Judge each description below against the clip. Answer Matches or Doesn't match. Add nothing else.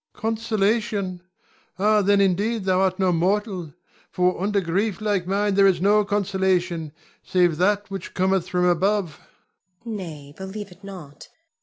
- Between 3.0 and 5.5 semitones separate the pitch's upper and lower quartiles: Doesn't match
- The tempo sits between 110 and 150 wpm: Matches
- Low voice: Doesn't match